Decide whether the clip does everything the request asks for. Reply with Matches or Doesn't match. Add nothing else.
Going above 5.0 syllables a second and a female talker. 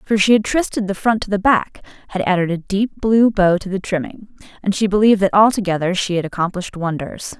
Matches